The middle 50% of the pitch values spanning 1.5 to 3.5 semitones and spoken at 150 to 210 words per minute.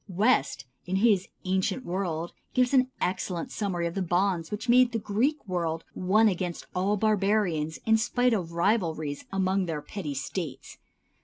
No: average, 4.1 semitones; average, 155 wpm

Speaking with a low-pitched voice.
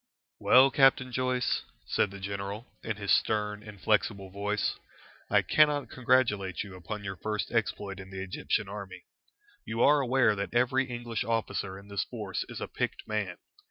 Yes: low, 105 Hz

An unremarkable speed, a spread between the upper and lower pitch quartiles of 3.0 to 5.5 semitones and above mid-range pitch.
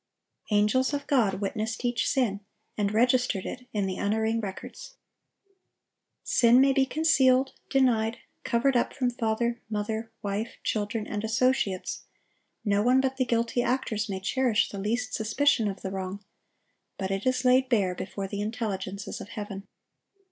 Yes: average, 150 wpm; average, 3.7 semitones; high, 225 Hz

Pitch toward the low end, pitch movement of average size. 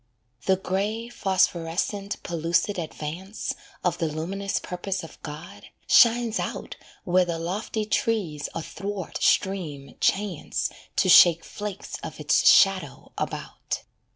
No: medium, 185 Hz; average, 3.5 semitones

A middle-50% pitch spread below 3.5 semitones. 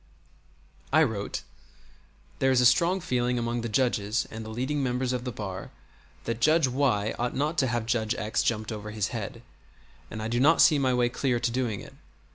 Yes: average, 3.0 semitones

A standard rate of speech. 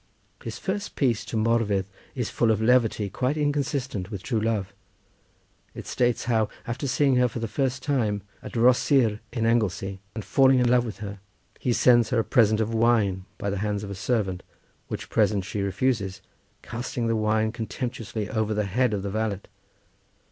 Yes: average, 180 wpm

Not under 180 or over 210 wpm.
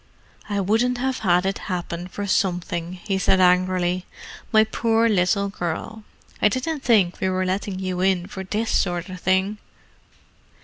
No: average, 160 wpm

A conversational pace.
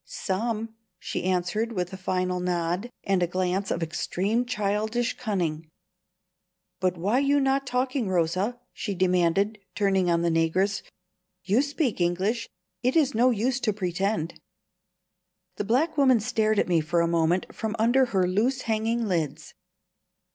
Yes: average, 145 wpm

